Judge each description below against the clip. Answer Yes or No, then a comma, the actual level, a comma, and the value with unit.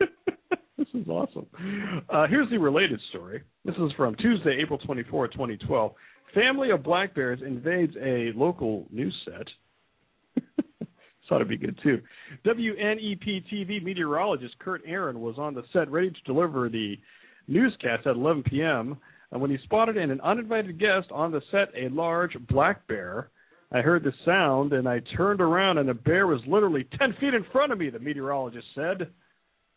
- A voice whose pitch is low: No, medium, 170 Hz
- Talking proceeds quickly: No, average, 165 wpm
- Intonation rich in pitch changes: Yes, wide, 7.1 semitones